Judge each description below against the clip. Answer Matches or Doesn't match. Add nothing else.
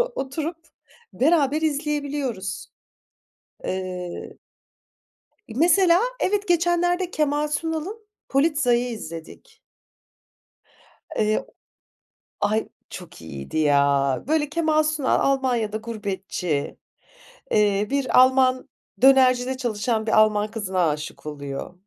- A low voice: Doesn't match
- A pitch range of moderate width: Doesn't match